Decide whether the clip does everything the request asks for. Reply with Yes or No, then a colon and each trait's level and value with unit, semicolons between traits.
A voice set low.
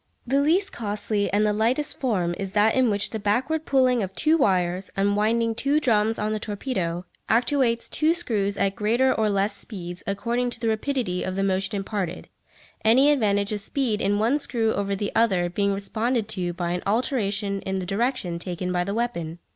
No: high, 210 Hz